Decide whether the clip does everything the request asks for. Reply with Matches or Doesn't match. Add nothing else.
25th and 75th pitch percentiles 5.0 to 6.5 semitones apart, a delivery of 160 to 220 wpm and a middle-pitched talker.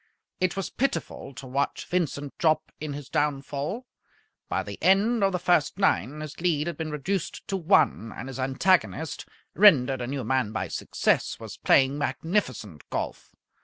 Matches